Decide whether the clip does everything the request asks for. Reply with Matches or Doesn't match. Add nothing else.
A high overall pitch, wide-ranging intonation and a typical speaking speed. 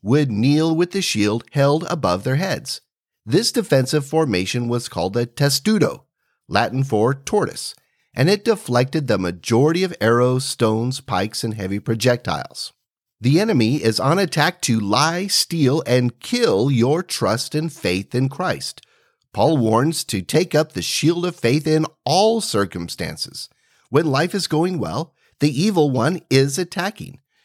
Doesn't match